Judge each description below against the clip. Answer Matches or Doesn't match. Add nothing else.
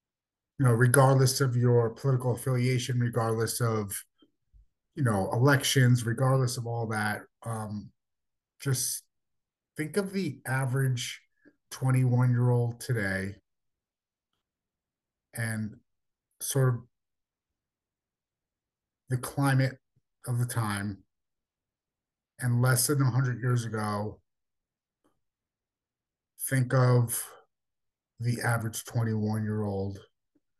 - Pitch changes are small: Doesn't match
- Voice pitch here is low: Matches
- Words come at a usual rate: Doesn't match